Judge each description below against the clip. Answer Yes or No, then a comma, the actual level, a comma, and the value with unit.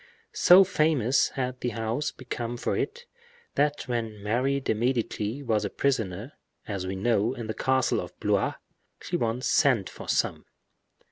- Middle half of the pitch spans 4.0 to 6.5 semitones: No, average, 3.6 semitones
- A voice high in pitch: No, low, 120 Hz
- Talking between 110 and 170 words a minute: Yes, average, 155 wpm